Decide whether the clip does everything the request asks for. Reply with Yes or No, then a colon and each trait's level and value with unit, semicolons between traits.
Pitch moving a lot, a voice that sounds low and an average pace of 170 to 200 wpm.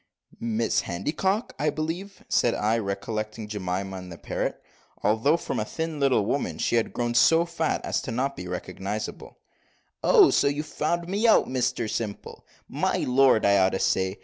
Yes: wide, 7.1 semitones; low, 115 Hz; average, 175 wpm